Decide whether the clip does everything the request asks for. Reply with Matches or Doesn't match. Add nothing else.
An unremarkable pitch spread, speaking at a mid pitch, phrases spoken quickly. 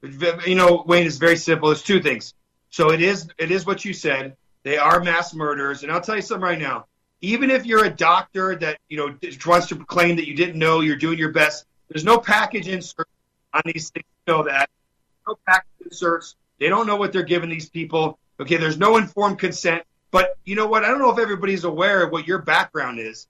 Matches